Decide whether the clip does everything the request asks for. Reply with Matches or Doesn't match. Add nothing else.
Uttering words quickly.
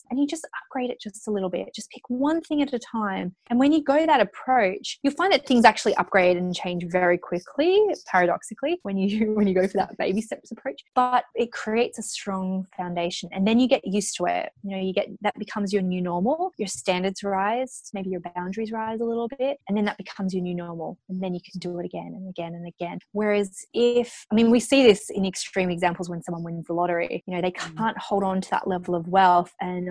Matches